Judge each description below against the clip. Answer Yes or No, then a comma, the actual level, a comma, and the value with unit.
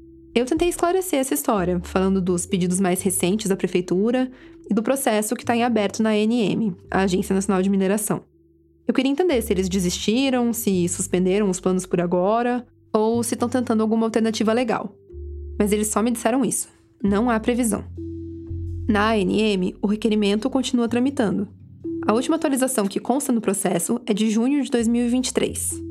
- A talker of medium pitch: No, high, 215 Hz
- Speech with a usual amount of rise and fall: Yes, average, 4.3 semitones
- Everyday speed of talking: Yes, average, 165 wpm